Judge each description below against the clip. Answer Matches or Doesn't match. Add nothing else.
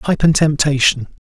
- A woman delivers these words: Doesn't match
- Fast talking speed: Doesn't match